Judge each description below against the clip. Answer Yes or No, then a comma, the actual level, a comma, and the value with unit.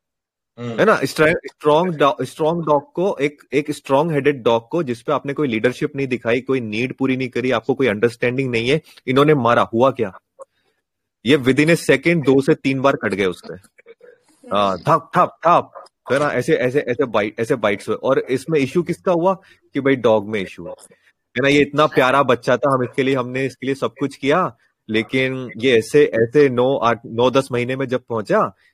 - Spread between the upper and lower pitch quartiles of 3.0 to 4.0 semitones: Yes, average, 3.3 semitones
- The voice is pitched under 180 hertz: Yes, low, 135 Hz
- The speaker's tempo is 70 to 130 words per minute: No, average, 160 wpm